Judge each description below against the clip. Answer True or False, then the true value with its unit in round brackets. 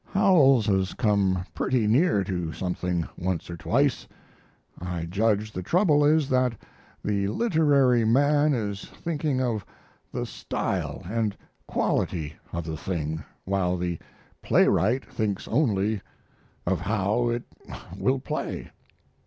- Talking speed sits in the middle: False (120 wpm)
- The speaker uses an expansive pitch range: True (6.1 semitones)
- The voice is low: True (105 Hz)